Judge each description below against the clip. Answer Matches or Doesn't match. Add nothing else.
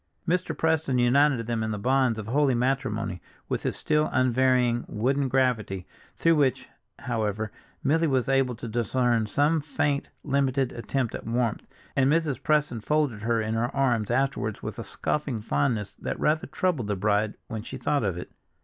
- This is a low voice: Matches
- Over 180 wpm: Doesn't match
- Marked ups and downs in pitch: Doesn't match